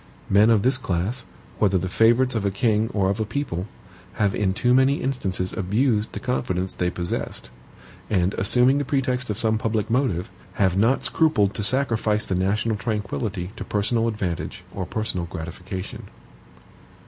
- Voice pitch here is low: Yes, low, 105 Hz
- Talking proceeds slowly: No, average, 160 wpm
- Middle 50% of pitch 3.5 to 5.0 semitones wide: Yes, average, 4.1 semitones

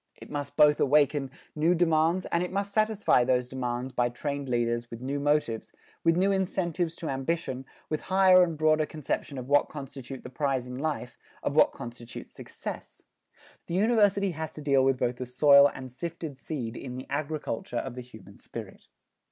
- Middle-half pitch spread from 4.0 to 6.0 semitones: Yes, average, 4.6 semitones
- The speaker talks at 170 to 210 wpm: Yes, average, 180 wpm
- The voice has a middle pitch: Yes, medium, 145 Hz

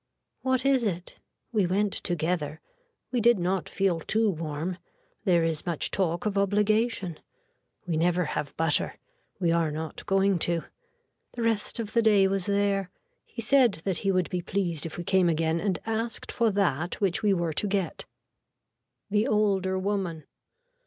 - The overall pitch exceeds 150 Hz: Yes, high, 190 Hz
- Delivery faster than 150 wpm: Yes, average, 165 wpm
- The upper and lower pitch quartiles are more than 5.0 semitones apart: No, average, 3.6 semitones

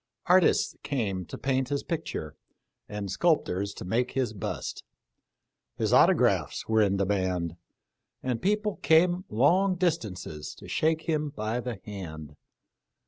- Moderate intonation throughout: No, wide, 8.6 semitones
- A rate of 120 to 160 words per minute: Yes, average, 140 wpm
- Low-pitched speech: Yes, low, 120 Hz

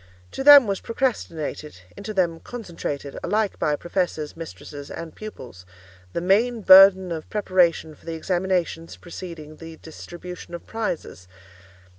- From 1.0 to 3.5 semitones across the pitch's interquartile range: No, average, 4.1 semitones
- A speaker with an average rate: No, slow, 120 wpm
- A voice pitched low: No, medium, 170 Hz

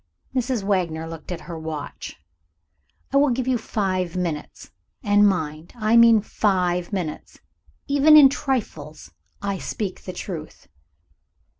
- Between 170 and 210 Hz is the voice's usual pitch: Yes, high, 190 Hz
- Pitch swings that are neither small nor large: No, wide, 5.8 semitones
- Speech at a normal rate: No, slow, 130 wpm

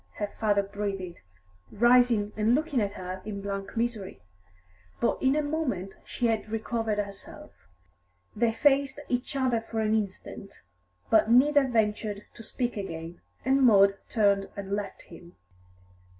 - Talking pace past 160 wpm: No, average, 140 wpm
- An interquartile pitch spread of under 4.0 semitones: Yes, average, 3.5 semitones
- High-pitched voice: Yes, high, 215 Hz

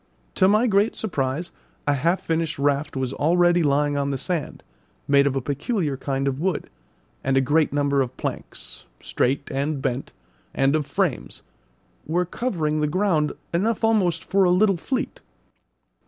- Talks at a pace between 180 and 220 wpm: No, average, 160 wpm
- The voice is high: No, medium, 150 Hz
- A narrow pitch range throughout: No, average, 4.4 semitones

